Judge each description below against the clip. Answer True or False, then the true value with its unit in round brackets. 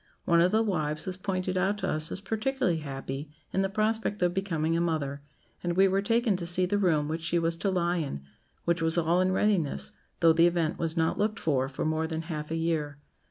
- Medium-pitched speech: True (170 Hz)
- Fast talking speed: True (230 wpm)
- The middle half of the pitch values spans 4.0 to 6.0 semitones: False (3.2 semitones)